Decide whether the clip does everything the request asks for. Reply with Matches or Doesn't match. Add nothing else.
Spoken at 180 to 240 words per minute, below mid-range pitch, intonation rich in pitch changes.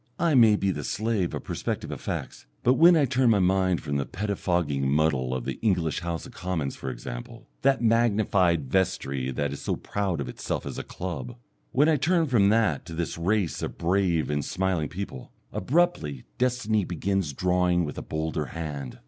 Matches